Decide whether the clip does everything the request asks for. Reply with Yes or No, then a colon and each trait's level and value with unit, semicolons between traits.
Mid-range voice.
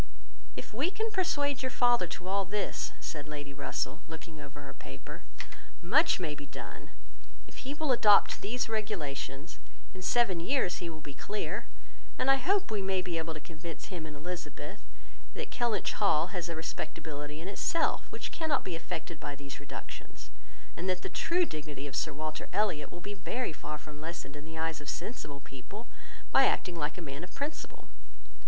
Yes: medium, 170 Hz